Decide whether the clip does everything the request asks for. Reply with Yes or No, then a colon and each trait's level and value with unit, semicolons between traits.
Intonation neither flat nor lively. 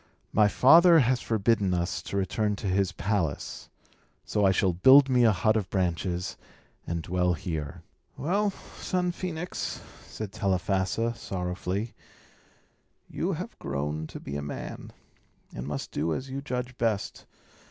No: wide, 5.8 semitones